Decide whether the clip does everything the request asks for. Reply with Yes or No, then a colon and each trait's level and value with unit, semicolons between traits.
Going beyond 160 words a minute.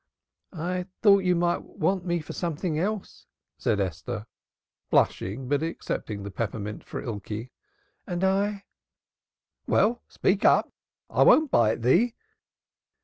No: slow, 135 wpm